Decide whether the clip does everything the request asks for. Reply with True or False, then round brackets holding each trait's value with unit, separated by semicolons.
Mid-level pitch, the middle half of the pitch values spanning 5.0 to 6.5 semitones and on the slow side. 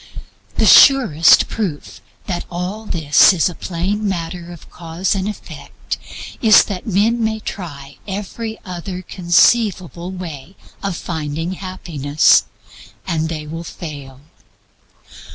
False (180 Hz; 3.5 semitones; 115 wpm)